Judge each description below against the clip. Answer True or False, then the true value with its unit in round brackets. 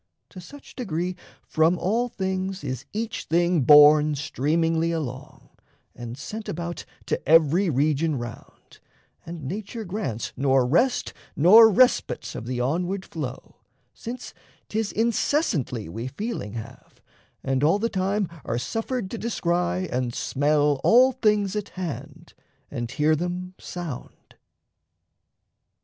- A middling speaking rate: False (125 wpm)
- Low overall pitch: False (170 Hz)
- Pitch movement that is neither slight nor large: False (6.5 semitones)